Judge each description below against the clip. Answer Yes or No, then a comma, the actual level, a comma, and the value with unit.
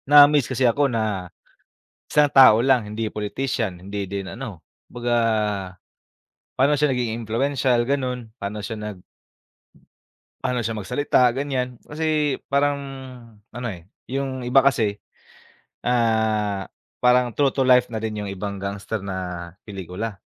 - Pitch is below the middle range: Yes, low, 120 Hz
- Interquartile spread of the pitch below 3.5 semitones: No, average, 4.3 semitones